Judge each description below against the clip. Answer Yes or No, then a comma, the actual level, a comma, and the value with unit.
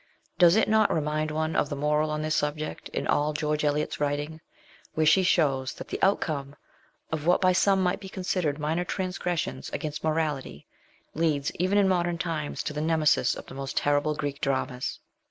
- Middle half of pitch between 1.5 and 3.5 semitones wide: Yes, average, 3.0 semitones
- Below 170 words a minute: No, average, 185 wpm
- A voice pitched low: No, medium, 155 Hz